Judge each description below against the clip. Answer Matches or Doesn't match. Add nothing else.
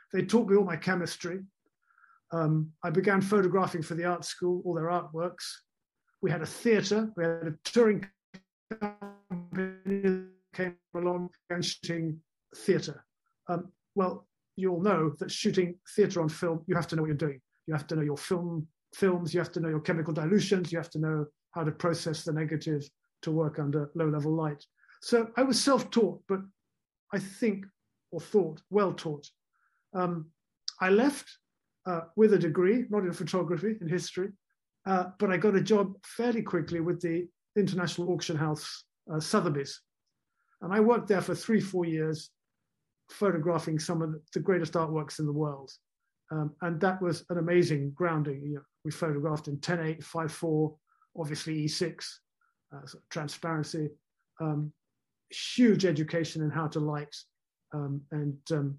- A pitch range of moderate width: Matches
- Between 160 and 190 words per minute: Matches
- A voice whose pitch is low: Doesn't match